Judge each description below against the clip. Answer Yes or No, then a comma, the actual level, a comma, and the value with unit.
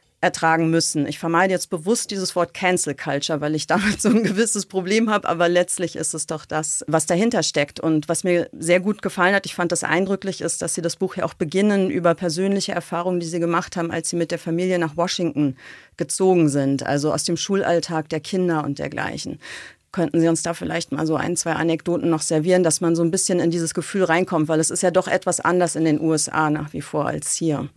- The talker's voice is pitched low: No, medium, 170 Hz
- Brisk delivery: Yes, fast, 230 wpm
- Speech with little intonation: Yes, narrow, 2.3 semitones